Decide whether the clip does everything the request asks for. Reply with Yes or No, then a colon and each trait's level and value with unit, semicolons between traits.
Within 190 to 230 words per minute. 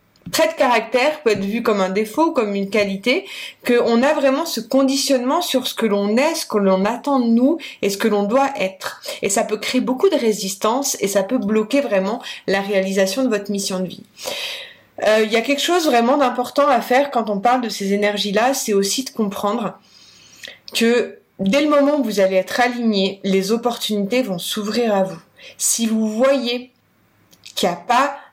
Yes: average, 200 wpm